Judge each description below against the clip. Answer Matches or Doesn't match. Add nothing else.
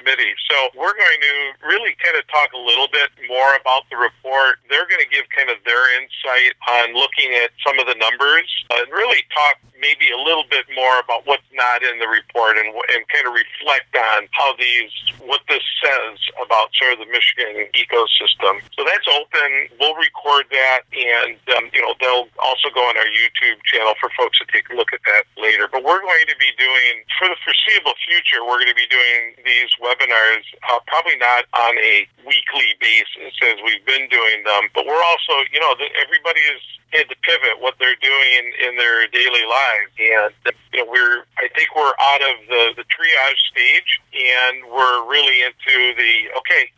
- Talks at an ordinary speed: Matches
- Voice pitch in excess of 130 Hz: Matches